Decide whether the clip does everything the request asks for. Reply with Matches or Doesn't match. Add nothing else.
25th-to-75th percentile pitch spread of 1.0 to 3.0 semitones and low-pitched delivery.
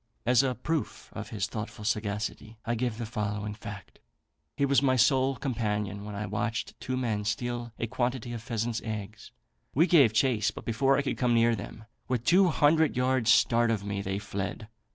Doesn't match